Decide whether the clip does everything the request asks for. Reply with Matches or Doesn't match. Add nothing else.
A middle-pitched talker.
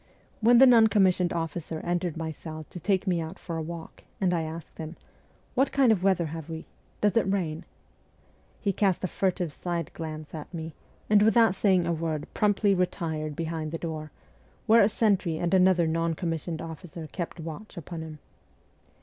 Matches